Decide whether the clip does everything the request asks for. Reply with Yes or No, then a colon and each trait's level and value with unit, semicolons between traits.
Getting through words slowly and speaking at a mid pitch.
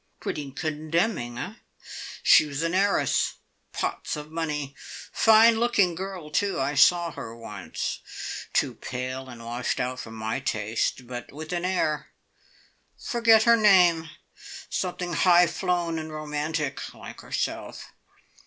Yes: slow, 130 wpm; medium, 155 Hz